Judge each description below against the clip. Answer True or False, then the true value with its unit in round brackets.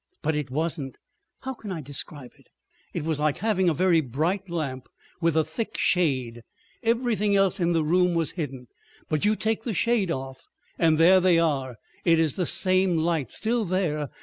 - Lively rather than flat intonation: False (4.1 semitones)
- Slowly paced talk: False (175 wpm)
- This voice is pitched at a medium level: True (165 Hz)